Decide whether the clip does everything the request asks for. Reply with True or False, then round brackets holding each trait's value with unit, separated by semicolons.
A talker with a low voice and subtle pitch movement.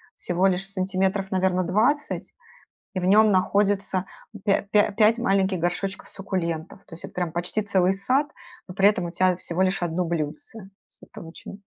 False (190 Hz; 1.9 semitones)